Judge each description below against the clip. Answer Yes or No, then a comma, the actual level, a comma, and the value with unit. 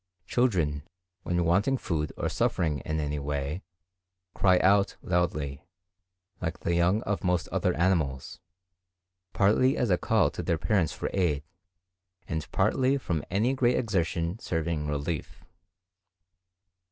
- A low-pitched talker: Yes, very low, 85 Hz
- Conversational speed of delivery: No, slow, 130 wpm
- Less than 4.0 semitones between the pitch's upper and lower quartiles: No, average, 4.4 semitones